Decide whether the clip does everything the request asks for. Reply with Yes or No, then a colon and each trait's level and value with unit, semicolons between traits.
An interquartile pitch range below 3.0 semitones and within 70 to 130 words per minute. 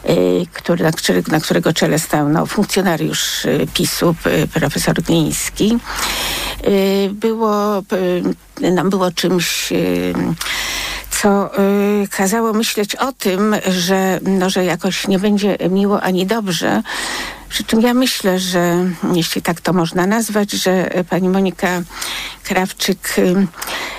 Yes: narrow, 2.4 semitones; average, 125 wpm